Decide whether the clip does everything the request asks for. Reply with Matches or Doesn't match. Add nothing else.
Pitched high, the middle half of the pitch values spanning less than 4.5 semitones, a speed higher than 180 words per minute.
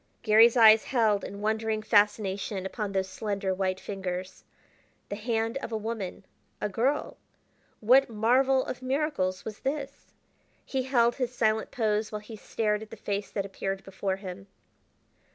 Doesn't match